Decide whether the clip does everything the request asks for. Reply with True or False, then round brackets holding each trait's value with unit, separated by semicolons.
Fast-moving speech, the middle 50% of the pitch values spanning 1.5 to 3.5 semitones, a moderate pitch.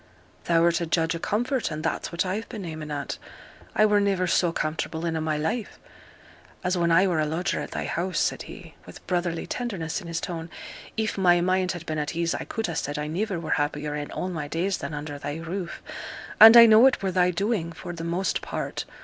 True (225 wpm; 3.1 semitones; 170 Hz)